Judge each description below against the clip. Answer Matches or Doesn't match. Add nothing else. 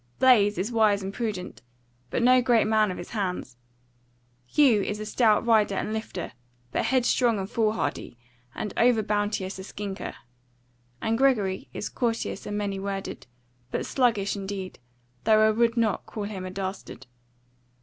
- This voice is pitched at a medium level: Doesn't match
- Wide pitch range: Doesn't match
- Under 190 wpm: Matches